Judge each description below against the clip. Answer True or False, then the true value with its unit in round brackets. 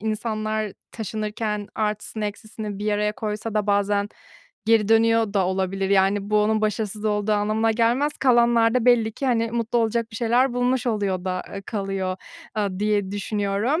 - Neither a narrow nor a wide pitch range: False (1.9 semitones)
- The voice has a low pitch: False (215 Hz)